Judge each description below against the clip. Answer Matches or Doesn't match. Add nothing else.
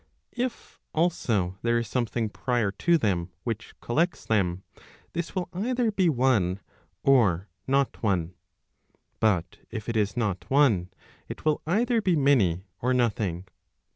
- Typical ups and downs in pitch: Doesn't match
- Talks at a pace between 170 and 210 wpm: Doesn't match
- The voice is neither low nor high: Doesn't match